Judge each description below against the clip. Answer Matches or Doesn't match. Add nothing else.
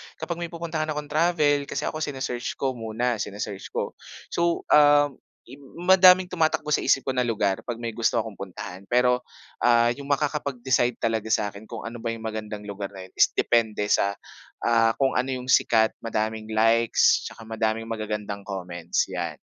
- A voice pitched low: Matches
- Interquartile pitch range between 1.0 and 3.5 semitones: Doesn't match